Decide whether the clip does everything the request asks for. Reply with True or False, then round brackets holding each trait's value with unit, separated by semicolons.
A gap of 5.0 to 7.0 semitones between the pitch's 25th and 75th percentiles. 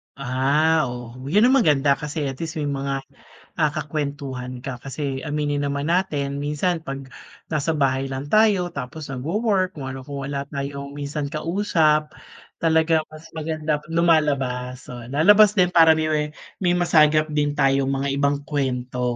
False (2.6 semitones)